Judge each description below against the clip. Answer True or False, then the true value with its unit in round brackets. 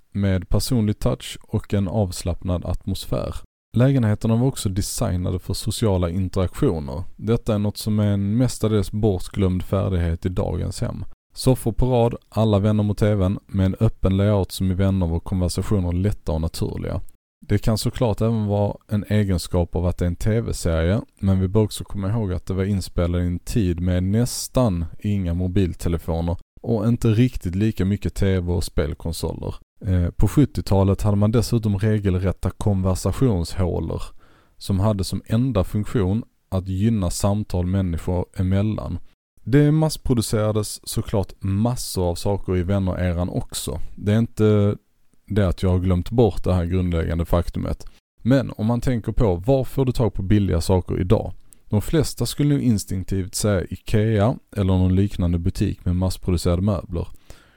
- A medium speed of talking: True (155 wpm)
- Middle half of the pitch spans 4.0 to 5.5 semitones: False (3.3 semitones)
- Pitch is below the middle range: True (100 Hz)